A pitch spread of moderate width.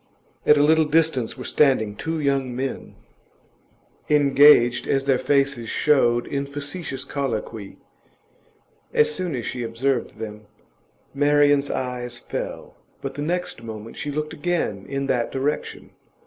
Yes: average, 3.5 semitones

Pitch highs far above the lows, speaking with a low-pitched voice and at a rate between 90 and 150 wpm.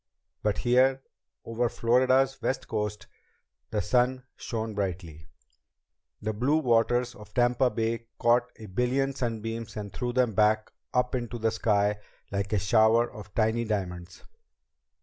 No: average, 2.7 semitones; low, 115 Hz; slow, 135 wpm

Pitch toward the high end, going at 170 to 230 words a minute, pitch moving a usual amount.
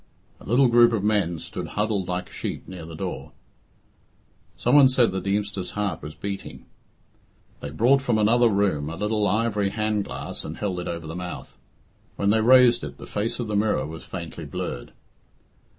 No: low, 105 Hz; average, 180 wpm; average, 4.0 semitones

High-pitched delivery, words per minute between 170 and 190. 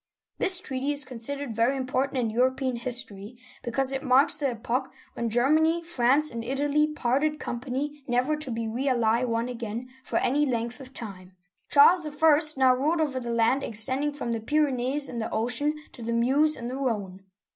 Yes: very high, 255 Hz; average, 180 wpm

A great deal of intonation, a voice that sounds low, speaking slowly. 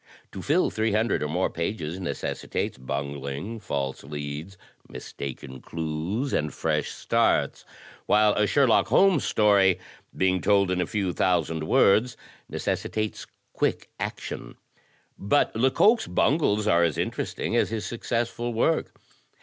Yes: wide, 6.4 semitones; very low, 95 Hz; slow, 130 wpm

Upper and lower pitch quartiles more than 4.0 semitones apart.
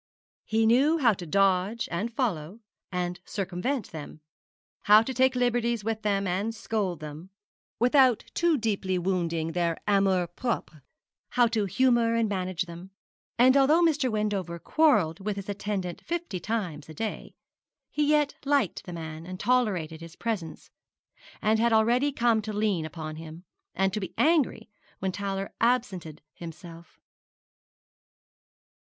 Yes: average, 5.2 semitones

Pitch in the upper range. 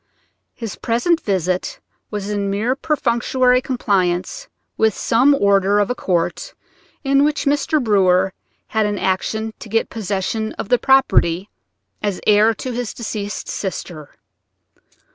Yes: high, 215 Hz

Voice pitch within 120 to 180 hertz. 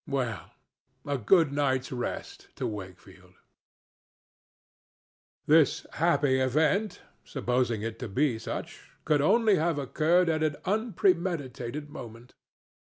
Yes: medium, 140 Hz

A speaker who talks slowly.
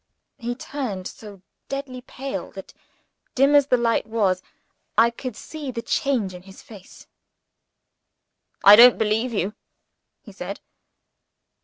Yes: slow, 130 wpm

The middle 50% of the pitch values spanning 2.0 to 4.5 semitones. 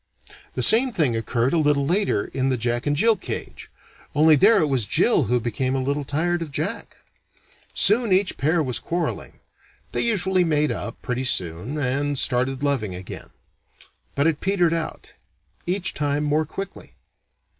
No: average, 5.2 semitones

